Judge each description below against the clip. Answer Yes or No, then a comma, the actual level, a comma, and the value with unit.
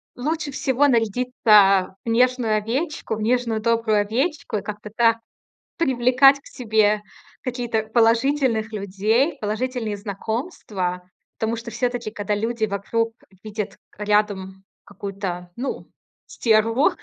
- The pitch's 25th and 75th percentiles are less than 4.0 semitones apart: Yes, average, 3.1 semitones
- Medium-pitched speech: No, high, 225 Hz